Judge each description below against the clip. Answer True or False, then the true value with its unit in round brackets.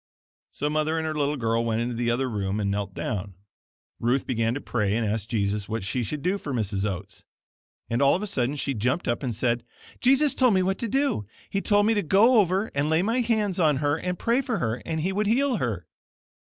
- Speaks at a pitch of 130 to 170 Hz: True (140 Hz)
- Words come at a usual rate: False (235 wpm)